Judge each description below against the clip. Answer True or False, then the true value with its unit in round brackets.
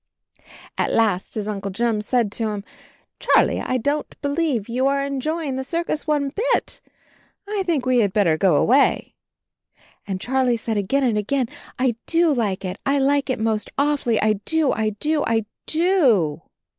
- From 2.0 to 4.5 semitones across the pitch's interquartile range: False (5.1 semitones)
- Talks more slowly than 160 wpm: False (170 wpm)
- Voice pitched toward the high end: True (255 Hz)